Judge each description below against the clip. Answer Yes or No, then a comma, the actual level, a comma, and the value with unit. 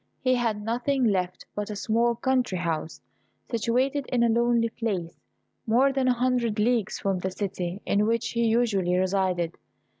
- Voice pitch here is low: No, high, 225 Hz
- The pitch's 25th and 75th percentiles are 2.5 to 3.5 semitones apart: No, average, 4.0 semitones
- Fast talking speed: No, average, 160 wpm